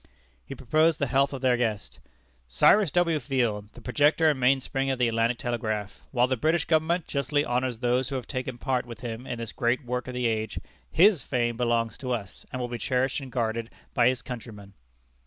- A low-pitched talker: Yes, low, 125 Hz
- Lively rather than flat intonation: No, narrow, 2.6 semitones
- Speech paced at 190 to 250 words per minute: Yes, fast, 205 wpm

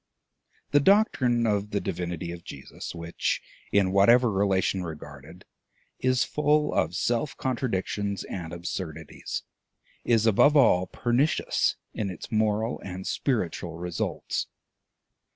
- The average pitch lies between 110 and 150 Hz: No, low, 100 Hz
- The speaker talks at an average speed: No, slow, 115 wpm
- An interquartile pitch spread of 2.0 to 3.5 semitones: No, wide, 5.4 semitones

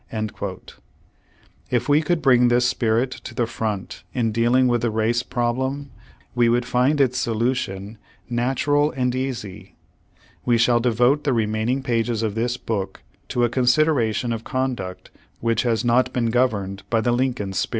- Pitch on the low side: Yes, low, 120 Hz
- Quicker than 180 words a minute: No, average, 160 wpm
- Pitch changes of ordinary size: No, narrow, 2.3 semitones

